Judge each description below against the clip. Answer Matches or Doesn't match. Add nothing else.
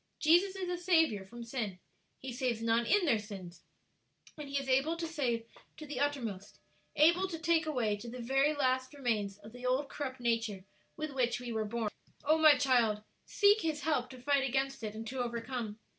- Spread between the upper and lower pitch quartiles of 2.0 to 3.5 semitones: Doesn't match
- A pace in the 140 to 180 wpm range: Doesn't match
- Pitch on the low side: Doesn't match